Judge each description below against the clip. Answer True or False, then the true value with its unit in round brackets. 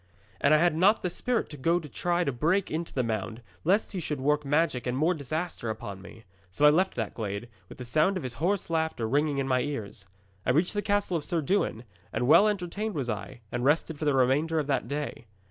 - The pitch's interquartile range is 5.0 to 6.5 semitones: True (5.6 semitones)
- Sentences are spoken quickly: True (235 wpm)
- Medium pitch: True (150 Hz)